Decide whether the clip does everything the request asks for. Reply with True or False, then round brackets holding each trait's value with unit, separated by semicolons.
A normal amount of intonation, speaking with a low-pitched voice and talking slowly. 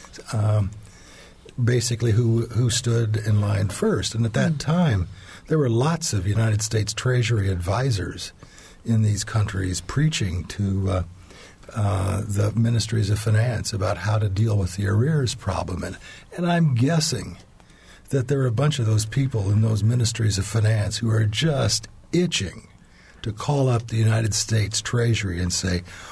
False (3.0 semitones; 110 Hz; 160 wpm)